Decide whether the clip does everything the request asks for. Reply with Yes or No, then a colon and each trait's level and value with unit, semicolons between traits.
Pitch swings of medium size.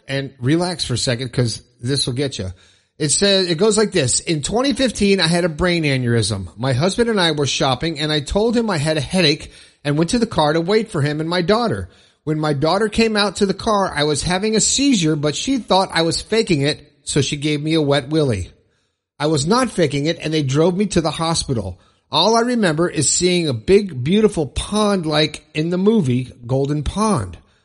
No: wide, 6.0 semitones